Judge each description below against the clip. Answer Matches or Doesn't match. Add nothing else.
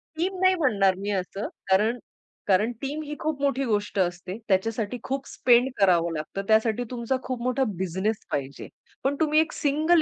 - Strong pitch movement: Matches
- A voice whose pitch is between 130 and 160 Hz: Doesn't match